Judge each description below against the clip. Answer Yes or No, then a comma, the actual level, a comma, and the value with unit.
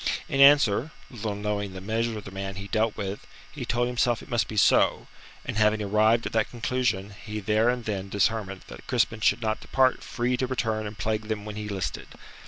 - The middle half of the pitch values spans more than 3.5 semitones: No, narrow, 2.4 semitones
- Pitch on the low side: Yes, low, 110 Hz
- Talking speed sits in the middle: No, fast, 210 wpm